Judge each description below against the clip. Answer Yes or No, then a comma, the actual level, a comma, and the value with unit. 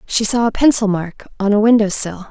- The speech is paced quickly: Yes, fast, 235 wpm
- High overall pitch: Yes, high, 210 Hz